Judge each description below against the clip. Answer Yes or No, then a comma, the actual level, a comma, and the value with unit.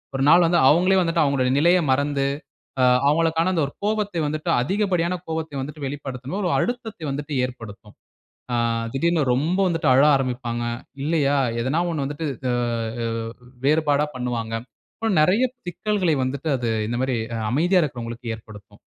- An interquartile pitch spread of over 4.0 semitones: Yes, average, 5.0 semitones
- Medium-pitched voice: Yes, medium, 145 Hz